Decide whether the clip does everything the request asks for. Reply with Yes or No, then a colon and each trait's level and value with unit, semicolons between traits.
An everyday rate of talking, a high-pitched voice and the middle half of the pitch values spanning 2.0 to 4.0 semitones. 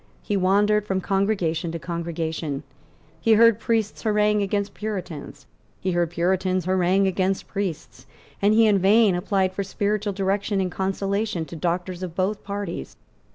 Yes: average, 150 wpm; high, 195 Hz; average, 2.7 semitones